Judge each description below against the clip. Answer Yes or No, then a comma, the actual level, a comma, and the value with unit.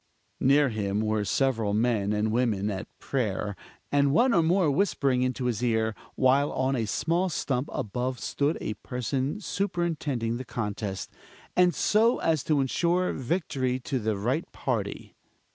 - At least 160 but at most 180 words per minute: No, average, 150 wpm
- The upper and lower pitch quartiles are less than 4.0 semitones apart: No, wide, 5.4 semitones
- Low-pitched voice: Yes, low, 130 Hz